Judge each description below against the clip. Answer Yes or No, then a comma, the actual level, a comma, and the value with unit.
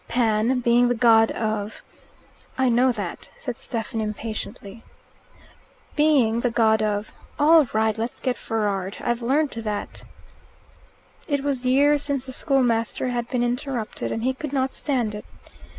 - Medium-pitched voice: No, high, 240 Hz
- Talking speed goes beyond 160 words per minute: No, average, 155 wpm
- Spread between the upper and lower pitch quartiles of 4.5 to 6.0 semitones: No, average, 3.0 semitones